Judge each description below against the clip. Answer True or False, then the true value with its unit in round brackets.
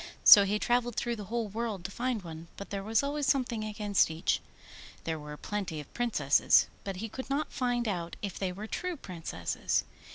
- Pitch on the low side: False (210 Hz)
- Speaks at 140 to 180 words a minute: False (195 wpm)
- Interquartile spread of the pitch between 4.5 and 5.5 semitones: True (4.8 semitones)